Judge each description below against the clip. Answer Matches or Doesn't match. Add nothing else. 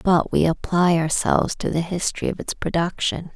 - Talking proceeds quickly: Doesn't match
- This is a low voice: Doesn't match